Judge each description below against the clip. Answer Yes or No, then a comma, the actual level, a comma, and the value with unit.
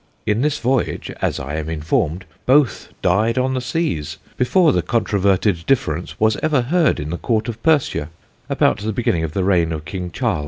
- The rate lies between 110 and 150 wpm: No, average, 190 wpm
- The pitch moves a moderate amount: No, wide, 7.3 semitones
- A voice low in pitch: Yes, low, 105 Hz